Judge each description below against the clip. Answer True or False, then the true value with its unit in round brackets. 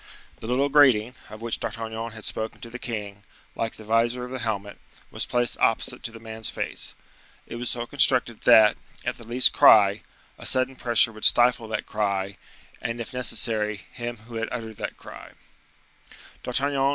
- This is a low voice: True (115 Hz)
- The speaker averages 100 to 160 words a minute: False (175 wpm)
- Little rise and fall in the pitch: True (2.0 semitones)